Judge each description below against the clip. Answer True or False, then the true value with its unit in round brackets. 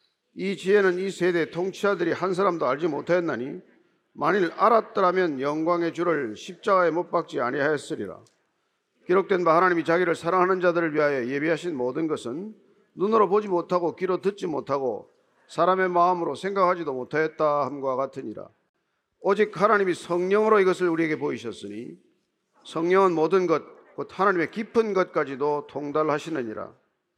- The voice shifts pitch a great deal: False (3.3 semitones)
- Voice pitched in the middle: True (175 Hz)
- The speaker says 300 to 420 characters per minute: True (355 characters per minute)